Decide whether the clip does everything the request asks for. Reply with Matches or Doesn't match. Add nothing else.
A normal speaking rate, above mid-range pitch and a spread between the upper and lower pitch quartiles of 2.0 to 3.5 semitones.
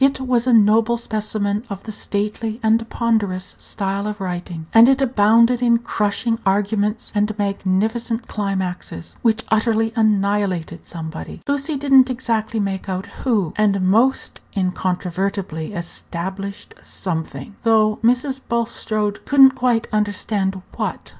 Doesn't match